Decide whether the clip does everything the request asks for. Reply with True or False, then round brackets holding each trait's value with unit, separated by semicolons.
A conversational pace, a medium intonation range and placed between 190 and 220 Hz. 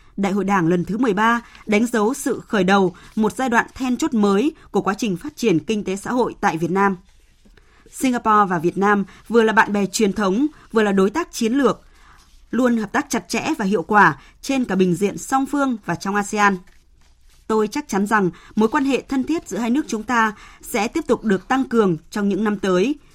True (225 wpm; 4.1 semitones; 215 Hz)